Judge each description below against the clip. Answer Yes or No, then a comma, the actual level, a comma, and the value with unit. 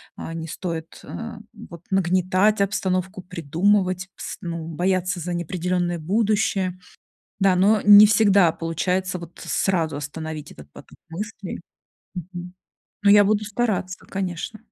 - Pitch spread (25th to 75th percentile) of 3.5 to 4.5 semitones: No, average, 2.8 semitones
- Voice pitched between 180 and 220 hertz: Yes, medium, 185 Hz